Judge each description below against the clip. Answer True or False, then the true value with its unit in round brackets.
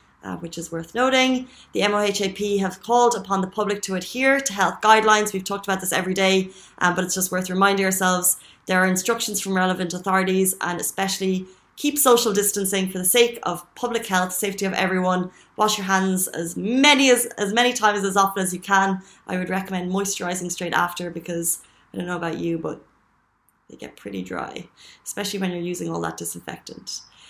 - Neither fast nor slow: False (195 wpm)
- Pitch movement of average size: False (2.1 semitones)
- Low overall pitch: False (190 Hz)